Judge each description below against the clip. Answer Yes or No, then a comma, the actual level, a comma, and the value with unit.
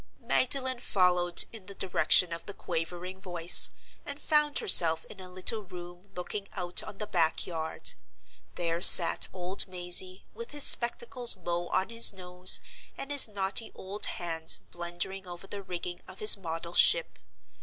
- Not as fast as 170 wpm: Yes, average, 155 wpm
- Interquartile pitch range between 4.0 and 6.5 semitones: No, average, 3.0 semitones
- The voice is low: No, medium, 185 Hz